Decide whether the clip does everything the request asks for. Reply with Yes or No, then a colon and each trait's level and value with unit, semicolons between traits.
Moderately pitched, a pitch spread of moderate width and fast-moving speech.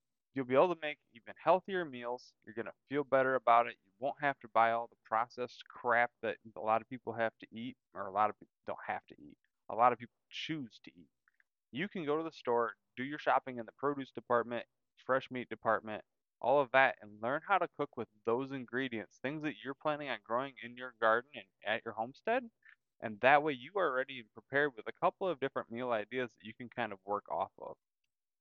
No: low, 125 Hz; average, 3.5 semitones; fast, 230 wpm